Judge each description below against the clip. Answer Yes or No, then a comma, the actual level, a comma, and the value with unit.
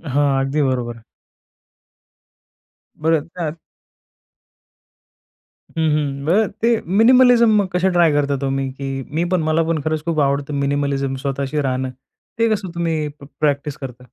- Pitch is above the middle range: No, medium, 150 Hz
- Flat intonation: No, average, 3.7 semitones